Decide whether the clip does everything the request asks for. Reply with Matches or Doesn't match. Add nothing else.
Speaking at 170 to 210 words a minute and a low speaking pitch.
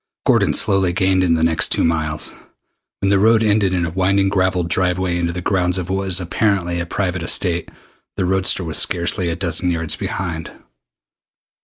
Matches